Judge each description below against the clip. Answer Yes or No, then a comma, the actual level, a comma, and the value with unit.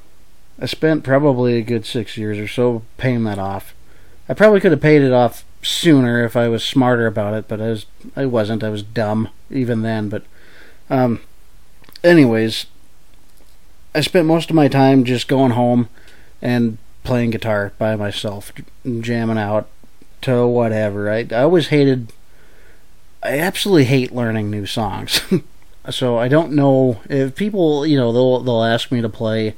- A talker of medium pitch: No, low, 120 Hz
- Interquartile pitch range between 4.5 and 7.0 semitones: No, average, 3.8 semitones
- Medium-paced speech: Yes, average, 165 wpm